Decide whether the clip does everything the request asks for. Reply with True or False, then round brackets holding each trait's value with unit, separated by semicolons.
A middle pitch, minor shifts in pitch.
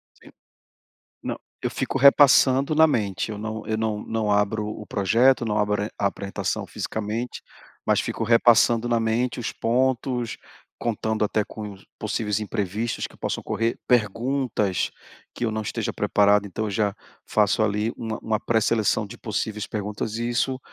False (110 Hz; 2.1 semitones)